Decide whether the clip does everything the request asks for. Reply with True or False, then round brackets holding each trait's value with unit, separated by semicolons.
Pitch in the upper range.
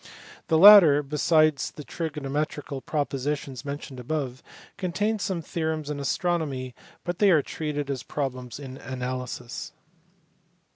False (145 Hz)